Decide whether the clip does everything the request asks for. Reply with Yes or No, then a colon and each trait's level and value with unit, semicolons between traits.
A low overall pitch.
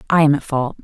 No: medium, 145 Hz